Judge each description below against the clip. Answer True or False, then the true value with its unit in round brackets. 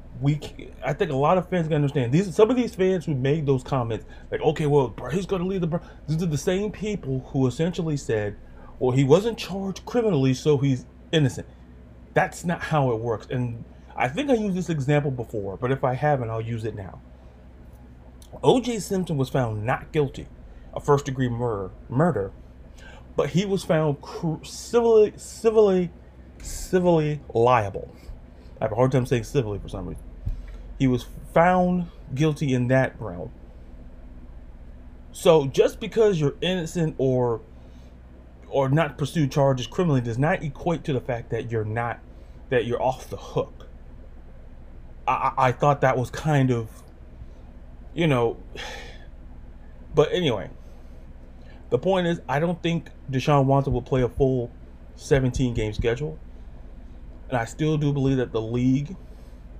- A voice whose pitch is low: True (125 Hz)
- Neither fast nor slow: True (160 wpm)